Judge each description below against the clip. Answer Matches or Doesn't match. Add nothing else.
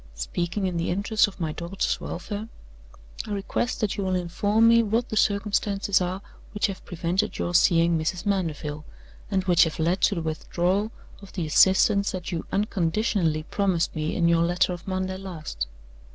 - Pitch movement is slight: Doesn't match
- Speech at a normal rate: Matches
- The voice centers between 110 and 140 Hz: Doesn't match